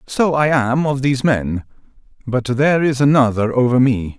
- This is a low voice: Yes, low, 130 Hz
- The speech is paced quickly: No, average, 170 wpm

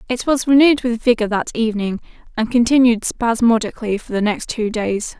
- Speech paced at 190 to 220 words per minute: No, average, 175 wpm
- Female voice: Yes, female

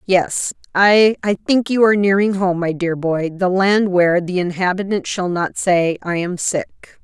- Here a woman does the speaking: Yes, female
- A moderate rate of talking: Yes, average, 180 wpm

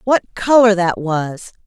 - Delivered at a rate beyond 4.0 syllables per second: No, 3.5 syllables/s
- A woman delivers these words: Yes, female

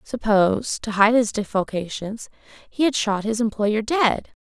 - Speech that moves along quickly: No, average, 150 wpm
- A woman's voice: Yes, female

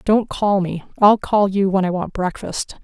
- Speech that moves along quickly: Yes, fast, 210 wpm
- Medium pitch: No, high, 195 Hz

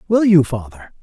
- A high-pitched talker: No, medium, 180 Hz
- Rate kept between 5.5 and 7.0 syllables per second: No, 5.1 syllables/s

